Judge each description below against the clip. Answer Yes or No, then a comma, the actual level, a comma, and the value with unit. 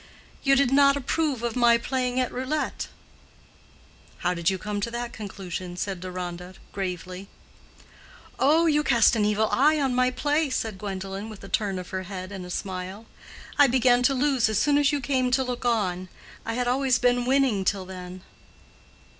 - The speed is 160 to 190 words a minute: Yes, average, 180 wpm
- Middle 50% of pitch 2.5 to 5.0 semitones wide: No, wide, 5.6 semitones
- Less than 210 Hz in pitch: No, high, 235 Hz